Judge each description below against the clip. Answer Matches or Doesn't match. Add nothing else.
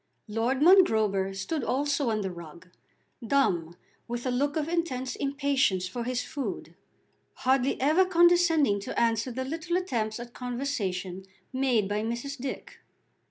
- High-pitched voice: Matches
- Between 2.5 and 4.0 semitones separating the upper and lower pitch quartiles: Doesn't match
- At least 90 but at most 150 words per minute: Matches